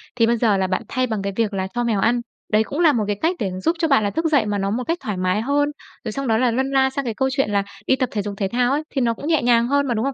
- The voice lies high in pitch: Yes, high, 240 Hz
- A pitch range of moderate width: Yes, average, 4.4 semitones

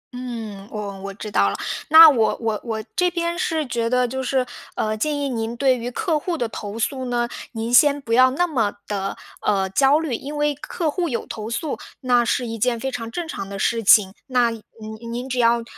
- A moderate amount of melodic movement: Yes, average, 4.0 semitones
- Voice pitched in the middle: No, high, 240 Hz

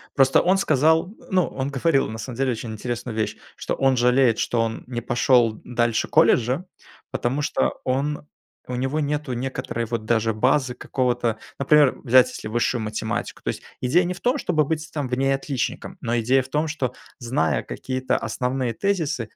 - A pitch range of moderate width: Yes, average, 3.7 semitones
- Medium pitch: No, low, 130 Hz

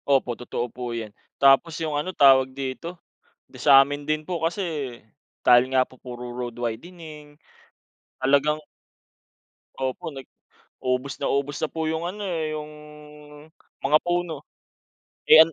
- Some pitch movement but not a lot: Yes, average, 3.6 semitones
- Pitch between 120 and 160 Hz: Yes, medium, 140 Hz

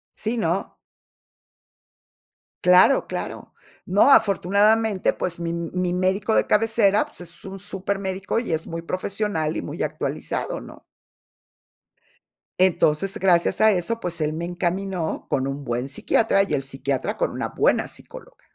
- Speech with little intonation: No, average, 3.2 semitones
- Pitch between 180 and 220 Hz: Yes, medium, 185 Hz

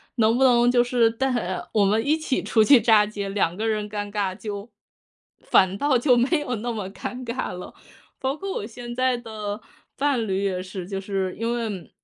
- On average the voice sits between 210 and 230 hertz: Yes, high, 220 Hz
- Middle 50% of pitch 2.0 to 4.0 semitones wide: Yes, average, 3.5 semitones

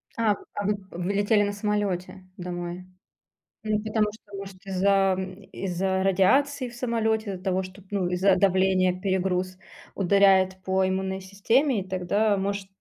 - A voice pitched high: Yes, high, 195 Hz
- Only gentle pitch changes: Yes, narrow, 1.8 semitones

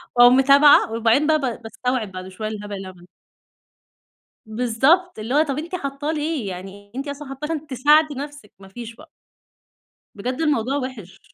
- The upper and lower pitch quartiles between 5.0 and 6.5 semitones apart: Yes, average, 5.3 semitones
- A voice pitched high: Yes, very high, 255 Hz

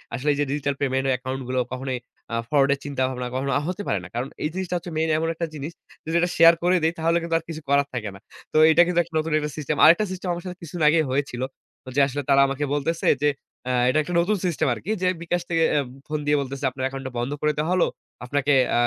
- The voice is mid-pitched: Yes, medium, 150 Hz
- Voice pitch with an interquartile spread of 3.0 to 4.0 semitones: Yes, average, 3.6 semitones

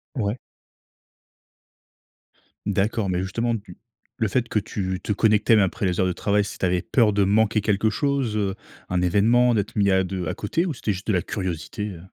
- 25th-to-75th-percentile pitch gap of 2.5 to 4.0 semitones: Yes, average, 2.8 semitones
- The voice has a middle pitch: No, low, 105 Hz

